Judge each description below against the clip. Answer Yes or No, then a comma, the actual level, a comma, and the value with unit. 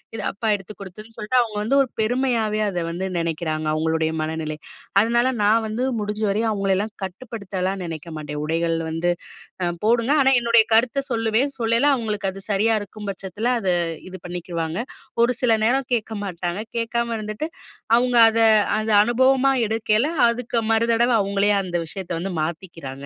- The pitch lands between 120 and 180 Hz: No, high, 210 Hz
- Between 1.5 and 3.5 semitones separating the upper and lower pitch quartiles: No, average, 4.7 semitones